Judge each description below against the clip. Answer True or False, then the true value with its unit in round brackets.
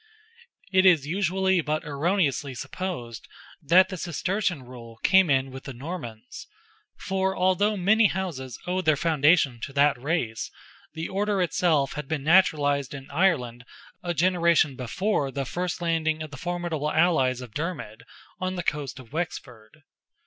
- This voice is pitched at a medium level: True (160 Hz)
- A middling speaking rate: True (150 wpm)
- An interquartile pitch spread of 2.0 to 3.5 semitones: False (5.1 semitones)